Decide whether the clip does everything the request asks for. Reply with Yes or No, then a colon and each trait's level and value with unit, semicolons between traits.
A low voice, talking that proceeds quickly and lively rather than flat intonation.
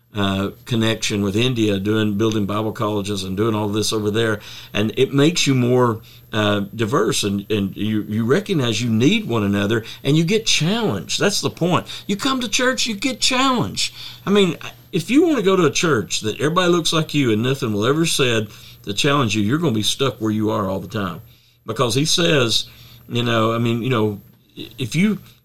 Yes: low, 120 Hz; fast, 210 wpm; wide, 5.9 semitones